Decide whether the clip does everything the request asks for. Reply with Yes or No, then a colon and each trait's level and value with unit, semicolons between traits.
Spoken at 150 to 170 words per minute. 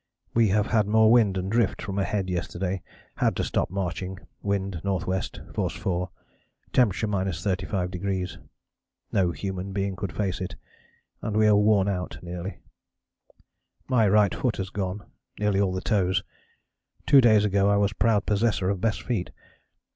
Yes: average, 155 wpm